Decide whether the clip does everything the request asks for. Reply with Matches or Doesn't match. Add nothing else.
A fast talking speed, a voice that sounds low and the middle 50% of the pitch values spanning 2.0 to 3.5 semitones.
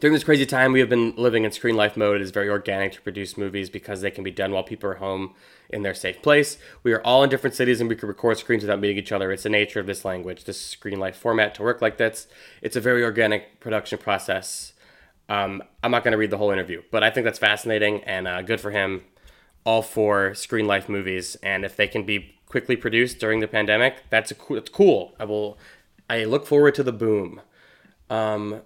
Matches